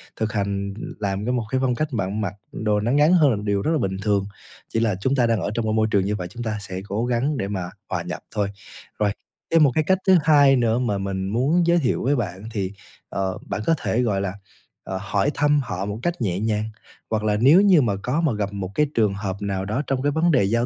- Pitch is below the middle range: Yes, low, 110 Hz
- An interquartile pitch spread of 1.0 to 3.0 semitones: No, average, 5.3 semitones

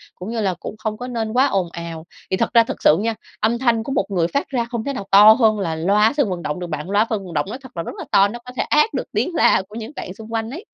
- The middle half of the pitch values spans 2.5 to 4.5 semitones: Yes, average, 4.1 semitones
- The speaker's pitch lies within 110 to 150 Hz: No, high, 215 Hz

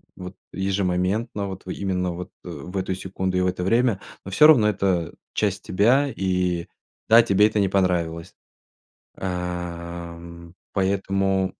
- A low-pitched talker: Yes, very low, 95 Hz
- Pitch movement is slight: Yes, narrow, 1.8 semitones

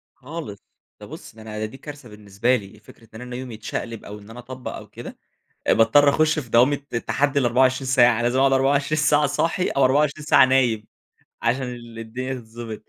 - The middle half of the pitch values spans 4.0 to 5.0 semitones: No, average, 3.5 semitones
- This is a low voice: Yes, low, 125 Hz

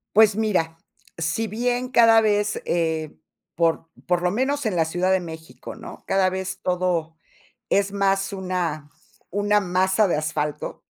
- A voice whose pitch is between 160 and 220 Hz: Yes, medium, 185 Hz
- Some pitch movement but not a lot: Yes, average, 4.0 semitones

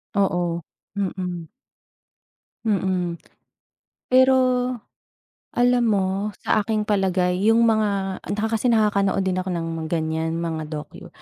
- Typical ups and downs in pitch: Yes, average, 3.8 semitones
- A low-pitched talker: No, high, 190 Hz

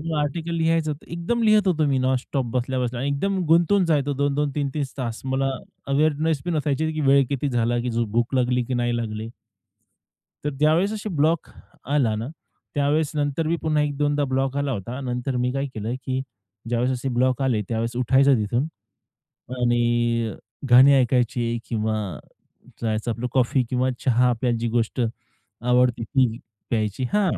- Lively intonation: No, average, 3.6 semitones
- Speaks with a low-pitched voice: Yes, low, 130 Hz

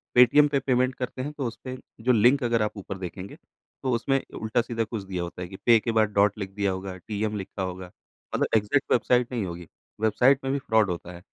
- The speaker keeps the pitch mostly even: No, average, 4.5 semitones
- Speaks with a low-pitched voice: Yes, low, 110 Hz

